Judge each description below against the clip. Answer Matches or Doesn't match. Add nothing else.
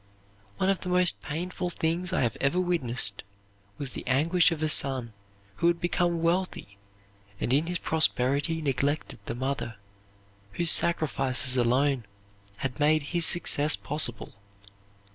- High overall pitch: Doesn't match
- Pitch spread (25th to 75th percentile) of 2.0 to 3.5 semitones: Doesn't match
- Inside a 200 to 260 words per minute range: Doesn't match